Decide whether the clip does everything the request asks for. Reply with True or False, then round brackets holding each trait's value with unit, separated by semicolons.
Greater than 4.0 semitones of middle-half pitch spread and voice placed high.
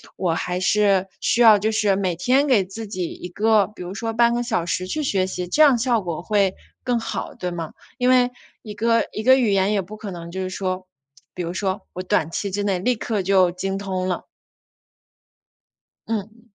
False (3.5 semitones; 200 Hz)